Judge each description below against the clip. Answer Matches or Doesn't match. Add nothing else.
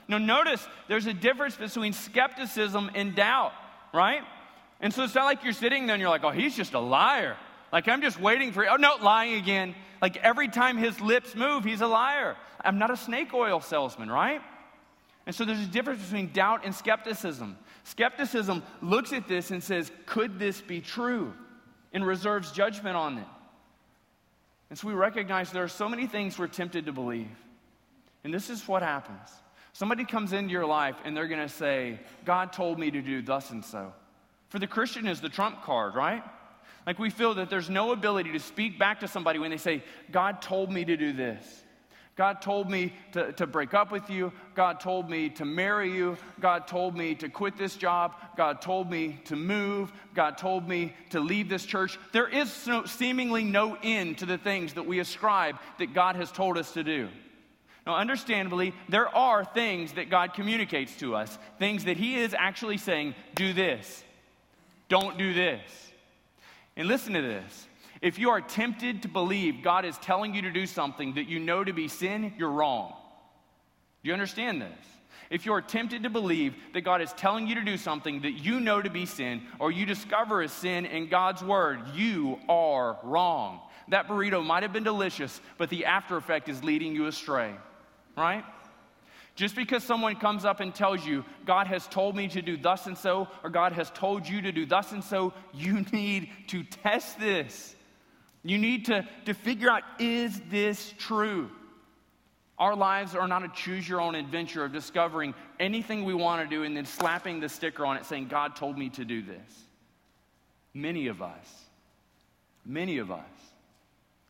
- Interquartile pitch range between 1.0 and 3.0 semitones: Doesn't match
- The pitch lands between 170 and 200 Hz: Matches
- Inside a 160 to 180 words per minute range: Doesn't match